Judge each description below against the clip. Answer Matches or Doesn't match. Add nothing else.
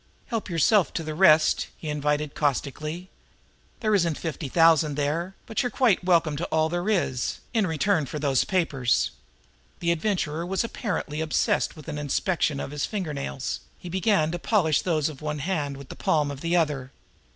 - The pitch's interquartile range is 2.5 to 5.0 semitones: Matches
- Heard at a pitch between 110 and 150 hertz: Doesn't match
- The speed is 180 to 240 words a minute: Matches